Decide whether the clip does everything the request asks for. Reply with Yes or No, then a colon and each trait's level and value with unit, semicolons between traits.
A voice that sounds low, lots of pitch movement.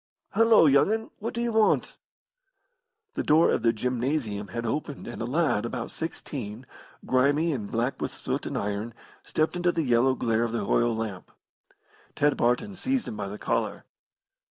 Yes: low, 130 Hz; wide, 6.2 semitones